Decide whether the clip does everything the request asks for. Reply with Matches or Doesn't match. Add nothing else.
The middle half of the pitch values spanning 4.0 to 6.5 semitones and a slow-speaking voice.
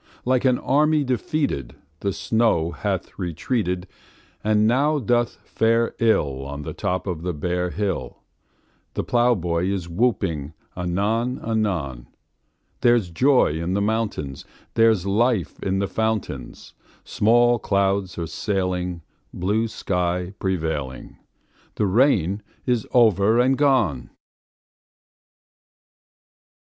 Matches